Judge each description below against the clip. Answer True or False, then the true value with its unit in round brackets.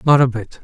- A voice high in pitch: False (125 Hz)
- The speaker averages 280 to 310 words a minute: True (285 wpm)